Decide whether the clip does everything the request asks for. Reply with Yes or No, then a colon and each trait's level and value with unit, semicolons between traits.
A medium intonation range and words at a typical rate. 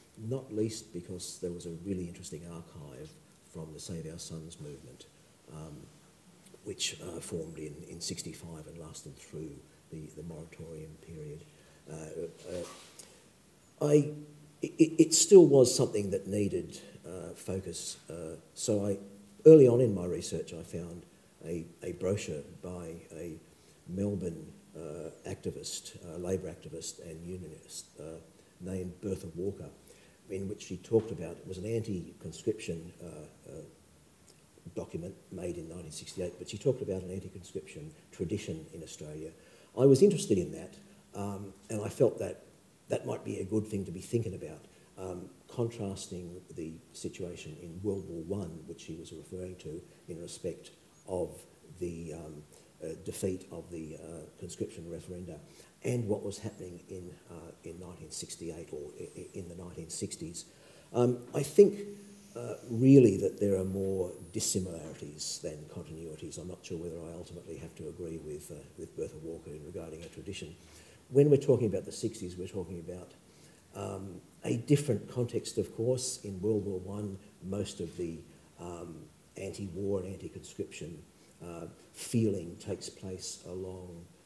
Yes: average, 3.9 semitones; average, 150 wpm